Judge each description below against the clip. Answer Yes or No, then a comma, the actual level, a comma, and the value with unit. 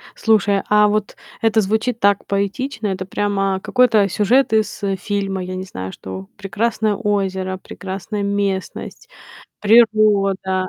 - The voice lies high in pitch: Yes, high, 200 Hz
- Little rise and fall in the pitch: Yes, narrow, 2.1 semitones